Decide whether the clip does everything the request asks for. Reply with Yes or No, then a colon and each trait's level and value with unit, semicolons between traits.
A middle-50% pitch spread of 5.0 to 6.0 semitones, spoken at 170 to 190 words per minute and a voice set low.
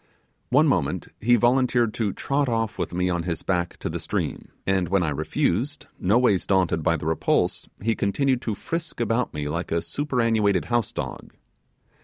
Yes: wide, 5.5 semitones; average, 175 wpm; low, 105 Hz